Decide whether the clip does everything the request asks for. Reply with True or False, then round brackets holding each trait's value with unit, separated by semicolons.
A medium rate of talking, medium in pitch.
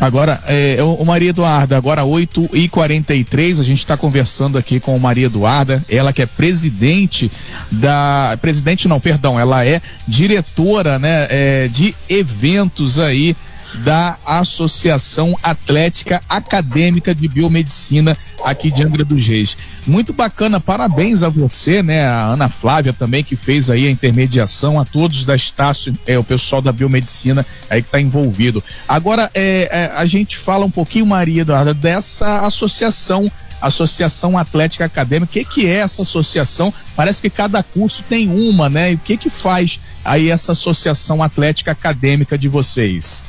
True (155 wpm; 155 Hz)